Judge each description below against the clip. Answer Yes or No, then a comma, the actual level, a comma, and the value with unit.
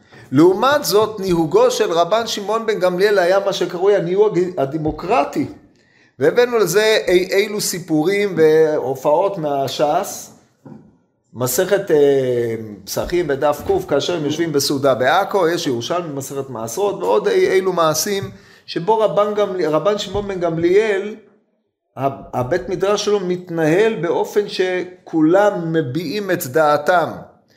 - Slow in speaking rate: No, average, 115 wpm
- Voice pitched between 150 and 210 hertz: Yes, medium, 185 Hz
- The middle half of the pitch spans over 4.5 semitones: Yes, average, 5.2 semitones